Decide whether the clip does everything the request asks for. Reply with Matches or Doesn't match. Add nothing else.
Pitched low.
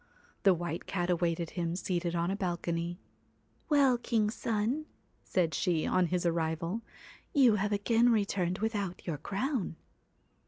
Doesn't match